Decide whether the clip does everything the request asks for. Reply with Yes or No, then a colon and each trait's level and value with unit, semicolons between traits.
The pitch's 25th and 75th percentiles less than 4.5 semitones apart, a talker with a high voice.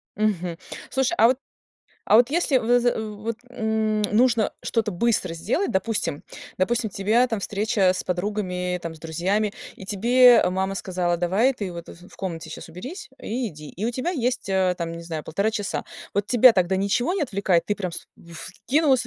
No: average, 4.8 semitones; high, 205 Hz